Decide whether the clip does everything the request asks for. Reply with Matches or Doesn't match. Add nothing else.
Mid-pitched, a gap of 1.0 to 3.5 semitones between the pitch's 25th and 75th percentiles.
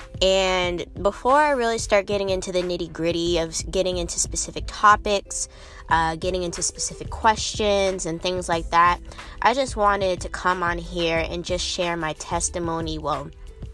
Matches